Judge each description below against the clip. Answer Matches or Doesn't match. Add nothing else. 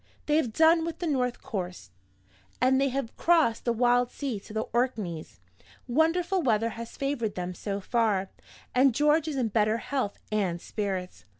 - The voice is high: Matches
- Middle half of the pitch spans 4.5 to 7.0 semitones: Matches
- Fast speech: Doesn't match